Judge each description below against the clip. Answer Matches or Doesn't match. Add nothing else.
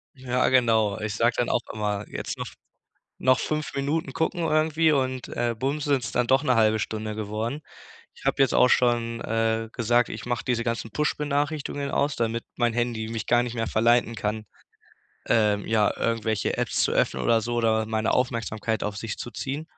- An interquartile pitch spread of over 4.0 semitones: Doesn't match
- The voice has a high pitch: Doesn't match